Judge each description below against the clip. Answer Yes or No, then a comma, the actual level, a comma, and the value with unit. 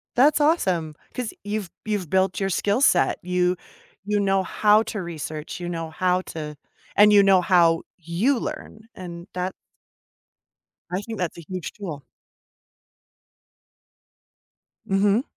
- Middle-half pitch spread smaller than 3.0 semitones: No, average, 3.4 semitones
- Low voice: No, medium, 185 Hz